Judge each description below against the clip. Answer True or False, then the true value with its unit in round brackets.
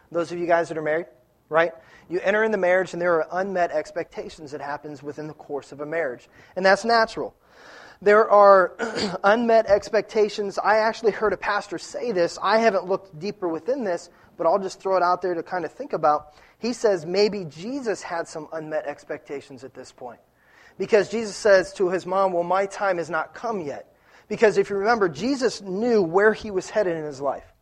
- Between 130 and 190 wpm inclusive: False (205 wpm)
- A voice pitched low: False (185 Hz)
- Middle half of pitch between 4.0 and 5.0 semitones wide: True (4.3 semitones)